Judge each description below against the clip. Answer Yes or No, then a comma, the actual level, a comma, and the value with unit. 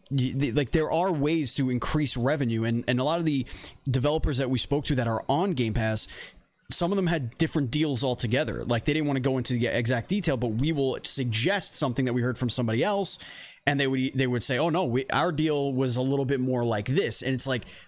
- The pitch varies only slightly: No, average, 3.4 semitones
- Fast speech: Yes, fast, 240 wpm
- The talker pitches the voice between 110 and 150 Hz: Yes, low, 130 Hz